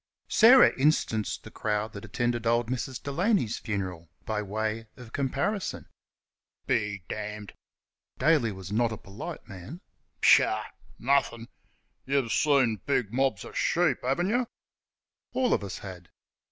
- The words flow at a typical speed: No, slow, 130 wpm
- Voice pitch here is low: Yes, low, 120 Hz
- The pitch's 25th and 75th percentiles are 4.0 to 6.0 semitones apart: Yes, average, 5.0 semitones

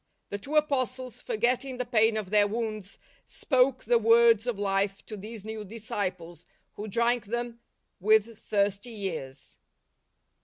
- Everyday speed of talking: Yes, average, 150 wpm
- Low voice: No, high, 220 Hz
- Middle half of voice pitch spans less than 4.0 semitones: Yes, average, 2.9 semitones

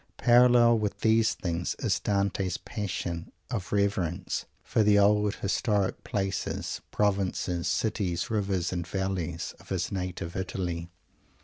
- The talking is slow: Yes, slow, 120 wpm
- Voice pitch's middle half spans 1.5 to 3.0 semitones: Yes, average, 2.7 semitones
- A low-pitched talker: Yes, very low, 95 Hz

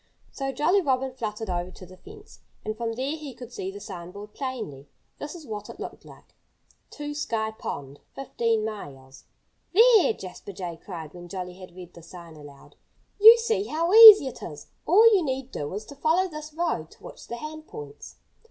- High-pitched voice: Yes, high, 225 Hz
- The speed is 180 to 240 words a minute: Yes, average, 195 wpm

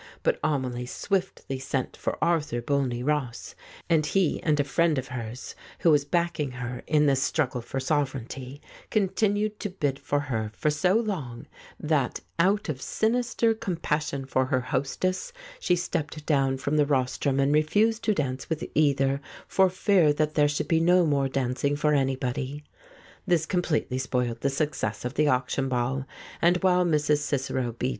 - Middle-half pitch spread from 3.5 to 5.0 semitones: Yes, average, 4.3 semitones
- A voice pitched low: No, medium, 145 Hz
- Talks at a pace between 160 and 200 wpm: Yes, average, 170 wpm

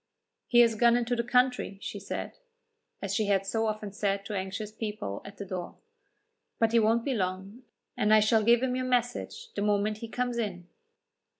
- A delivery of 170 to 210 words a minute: Yes, average, 195 wpm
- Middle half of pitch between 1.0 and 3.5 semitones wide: Yes, average, 2.8 semitones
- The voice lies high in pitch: Yes, high, 215 Hz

